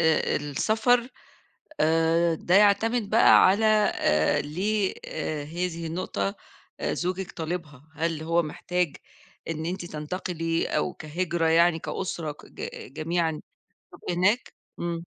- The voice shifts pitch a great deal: No, average, 2.7 semitones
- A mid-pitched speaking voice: Yes, medium, 170 Hz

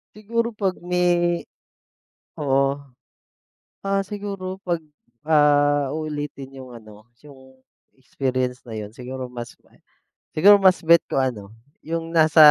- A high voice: No, medium, 150 Hz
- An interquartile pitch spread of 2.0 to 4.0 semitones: No, average, 5.2 semitones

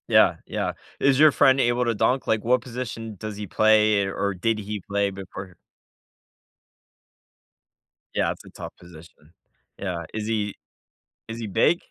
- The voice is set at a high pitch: No, low, 110 Hz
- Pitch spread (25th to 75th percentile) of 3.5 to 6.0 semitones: No, average, 3.1 semitones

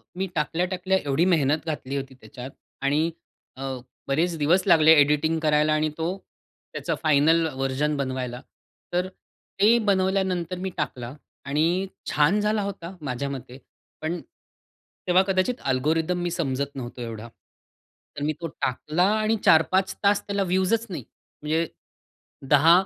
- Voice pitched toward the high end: No, medium, 160 Hz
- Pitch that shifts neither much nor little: Yes, average, 4.7 semitones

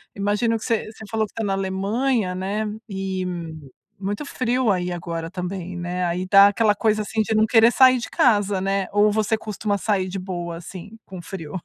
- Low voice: No, high, 200 Hz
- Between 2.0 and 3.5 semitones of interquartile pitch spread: Yes, average, 2.9 semitones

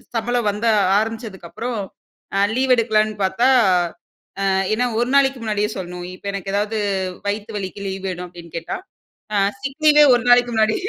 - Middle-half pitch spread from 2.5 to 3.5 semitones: No, average, 3.9 semitones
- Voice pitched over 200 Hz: Yes, high, 215 Hz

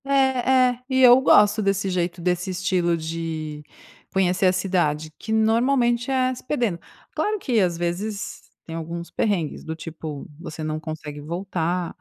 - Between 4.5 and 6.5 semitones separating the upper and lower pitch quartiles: Yes, average, 5.1 semitones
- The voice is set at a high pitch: No, medium, 180 Hz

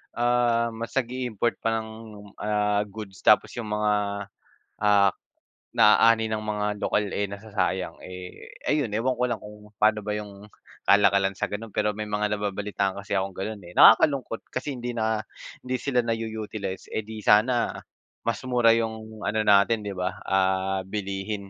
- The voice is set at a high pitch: No, low, 105 Hz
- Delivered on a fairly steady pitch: Yes, narrow, 2.2 semitones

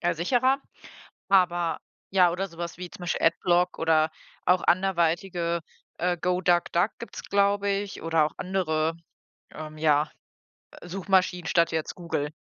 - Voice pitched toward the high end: No, medium, 175 Hz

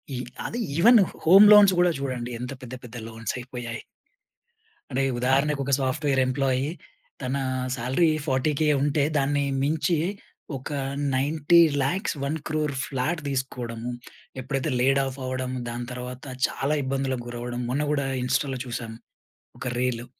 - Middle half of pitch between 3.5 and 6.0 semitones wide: No, average, 2.8 semitones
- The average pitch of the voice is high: No, low, 135 Hz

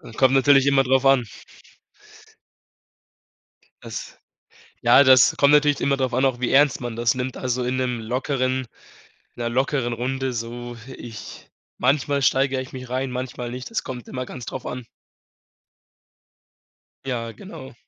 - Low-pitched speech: Yes, low, 130 Hz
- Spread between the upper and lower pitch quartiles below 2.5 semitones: Yes, narrow, 1.7 semitones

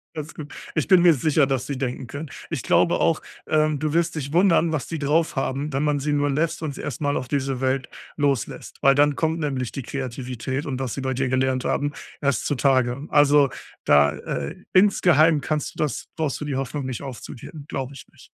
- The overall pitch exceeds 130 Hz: Yes, medium, 140 Hz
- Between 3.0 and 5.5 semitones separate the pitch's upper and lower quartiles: No, narrow, 2.6 semitones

